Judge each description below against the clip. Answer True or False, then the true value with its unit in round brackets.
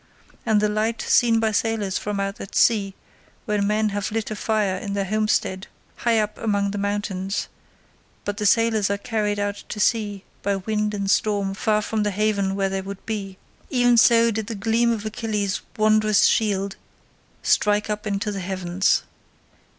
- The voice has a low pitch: False (210 Hz)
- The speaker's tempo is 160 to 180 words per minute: True (175 wpm)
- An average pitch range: False (1.6 semitones)